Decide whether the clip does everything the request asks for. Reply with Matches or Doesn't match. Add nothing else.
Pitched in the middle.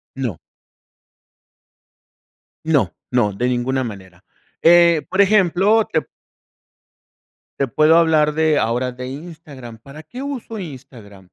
Matches